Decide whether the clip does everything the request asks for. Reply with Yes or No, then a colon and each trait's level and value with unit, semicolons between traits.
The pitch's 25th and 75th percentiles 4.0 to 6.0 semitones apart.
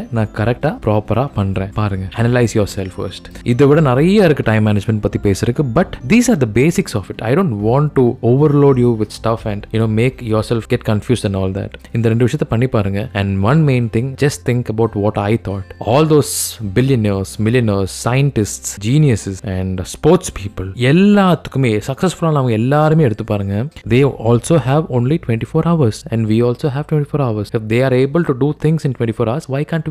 Yes: average, 5.2 semitones